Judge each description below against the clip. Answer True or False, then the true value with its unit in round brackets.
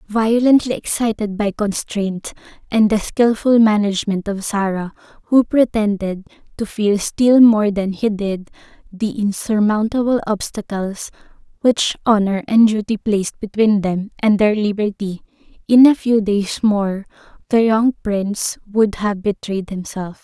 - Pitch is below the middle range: False (210 Hz)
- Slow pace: True (130 wpm)